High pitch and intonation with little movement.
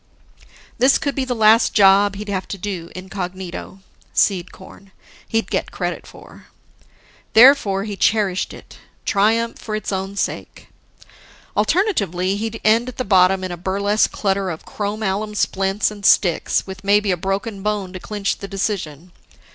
Yes: high, 200 Hz; narrow, 2.1 semitones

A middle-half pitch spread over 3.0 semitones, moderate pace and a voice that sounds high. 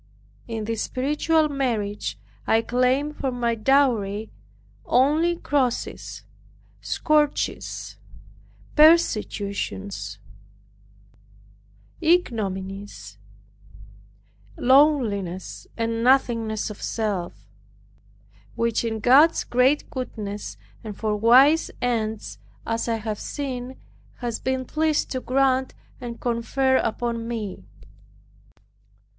No: average, 3.9 semitones; slow, 85 wpm; high, 235 Hz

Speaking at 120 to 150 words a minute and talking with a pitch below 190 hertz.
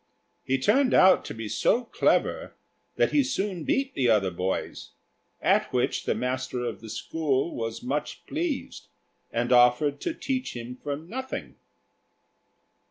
Yes: average, 145 wpm; low, 135 Hz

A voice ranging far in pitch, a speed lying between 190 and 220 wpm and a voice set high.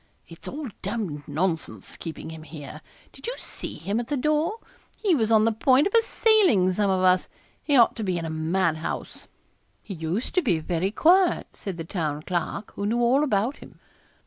Yes: wide, 7.8 semitones; average, 200 wpm; high, 200 Hz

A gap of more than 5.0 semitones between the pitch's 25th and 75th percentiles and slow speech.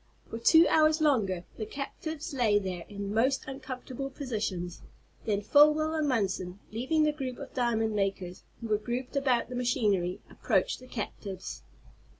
No: wide, 5.4 semitones; average, 150 wpm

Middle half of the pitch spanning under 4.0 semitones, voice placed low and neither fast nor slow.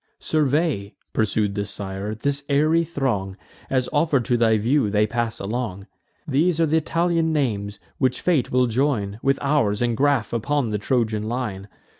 No: wide, 5.6 semitones; low, 125 Hz; average, 160 wpm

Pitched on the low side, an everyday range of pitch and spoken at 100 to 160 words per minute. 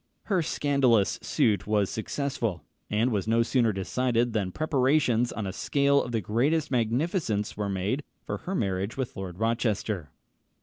Yes: low, 115 Hz; average, 4.7 semitones; average, 150 wpm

